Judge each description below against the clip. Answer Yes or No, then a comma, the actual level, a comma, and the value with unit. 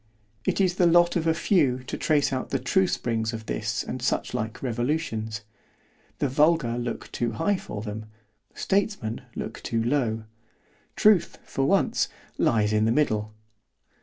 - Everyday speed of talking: Yes, average, 145 wpm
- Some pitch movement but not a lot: No, wide, 6.3 semitones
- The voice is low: Yes, low, 120 Hz